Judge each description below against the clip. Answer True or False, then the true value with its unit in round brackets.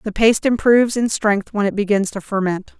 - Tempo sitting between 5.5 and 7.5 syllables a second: True (5.6 syllables/s)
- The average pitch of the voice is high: True (210 Hz)